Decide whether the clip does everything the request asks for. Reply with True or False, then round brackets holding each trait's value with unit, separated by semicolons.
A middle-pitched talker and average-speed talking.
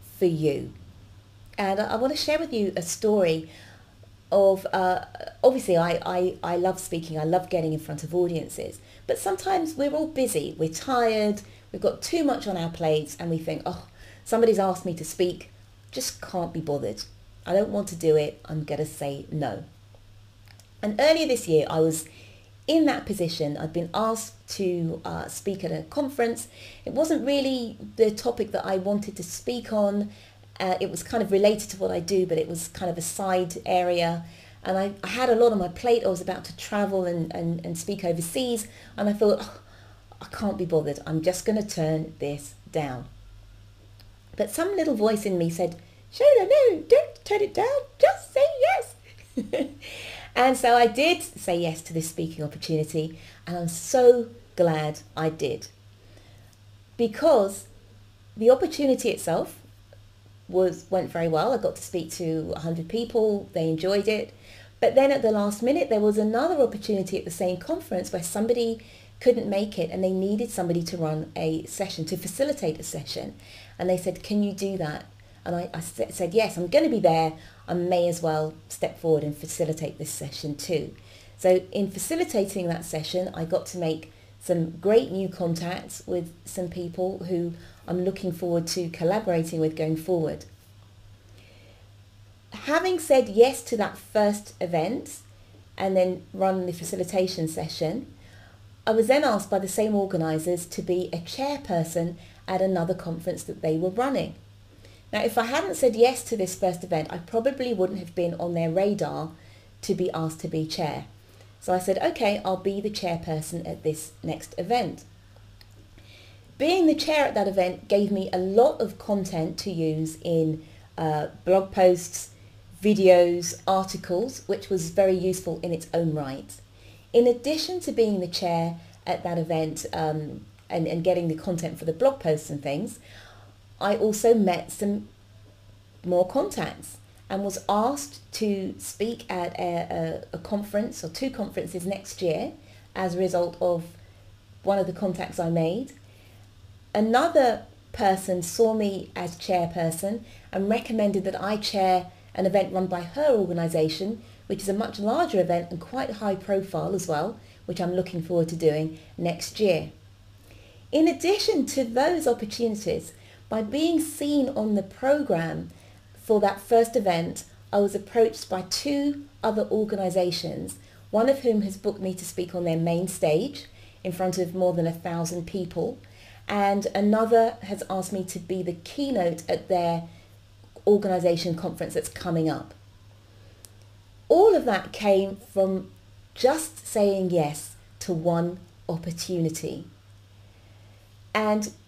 True (175 Hz; 165 wpm)